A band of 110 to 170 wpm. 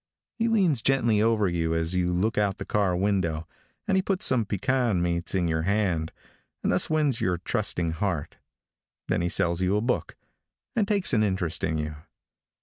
No: average, 185 wpm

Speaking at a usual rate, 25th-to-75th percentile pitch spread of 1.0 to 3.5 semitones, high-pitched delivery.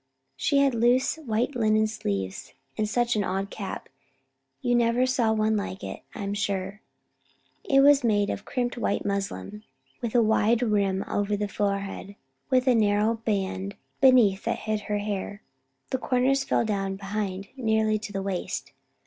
Yes: average, 165 wpm; average, 3.1 semitones; high, 215 Hz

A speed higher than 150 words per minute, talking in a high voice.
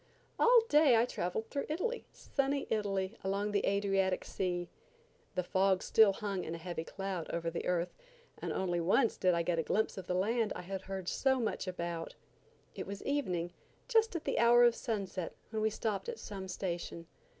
Yes: average, 185 wpm; high, 195 Hz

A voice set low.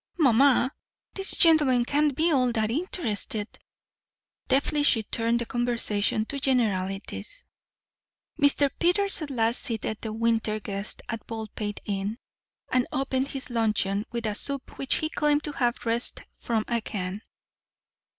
No: high, 235 Hz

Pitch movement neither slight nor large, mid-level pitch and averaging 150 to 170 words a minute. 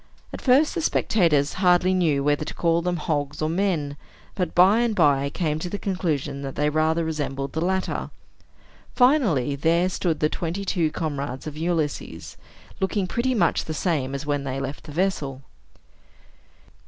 Yes: average, 4.3 semitones; medium, 160 Hz; average, 165 wpm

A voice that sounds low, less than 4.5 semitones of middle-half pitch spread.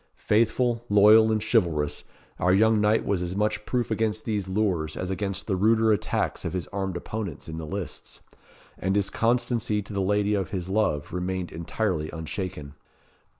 Yes: low, 100 Hz; average, 3.2 semitones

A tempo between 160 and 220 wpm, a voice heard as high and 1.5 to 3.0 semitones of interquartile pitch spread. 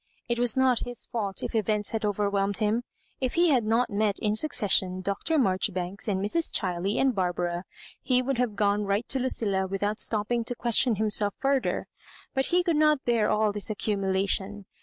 No: average, 195 wpm; high, 210 Hz; average, 3.6 semitones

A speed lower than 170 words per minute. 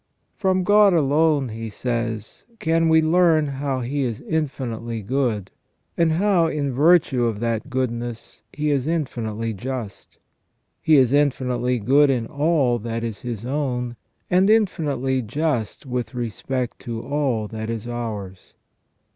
Yes: average, 140 wpm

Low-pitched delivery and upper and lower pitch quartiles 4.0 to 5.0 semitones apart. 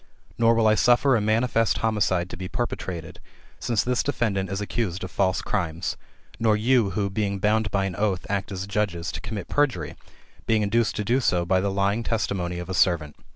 No: low, 100 Hz; average, 3.3 semitones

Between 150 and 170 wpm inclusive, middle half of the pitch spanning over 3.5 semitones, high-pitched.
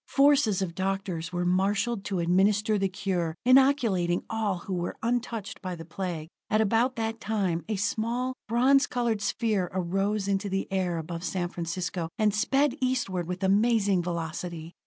Yes: average, 155 wpm; average, 4.0 semitones; high, 195 Hz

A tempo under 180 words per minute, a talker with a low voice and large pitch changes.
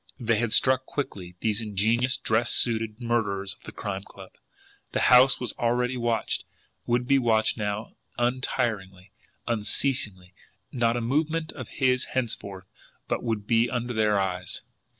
No: average, 145 wpm; low, 115 Hz; average, 3.2 semitones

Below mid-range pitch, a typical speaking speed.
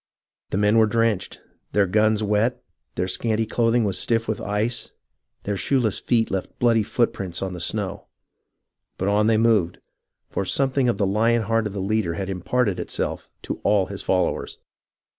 Yes: low, 105 Hz; average, 170 wpm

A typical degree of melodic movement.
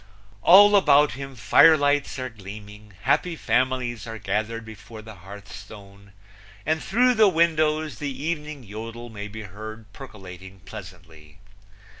No: wide, 6.3 semitones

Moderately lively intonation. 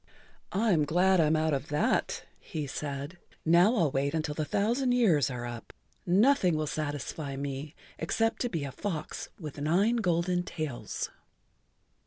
Yes: average, 4.4 semitones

